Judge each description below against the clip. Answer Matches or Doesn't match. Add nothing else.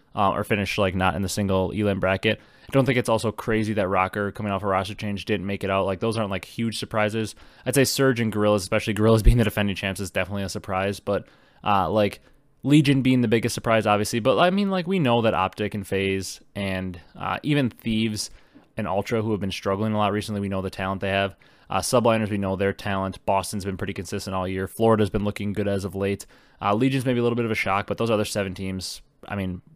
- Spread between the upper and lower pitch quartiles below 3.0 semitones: Matches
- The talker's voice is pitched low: Matches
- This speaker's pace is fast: Matches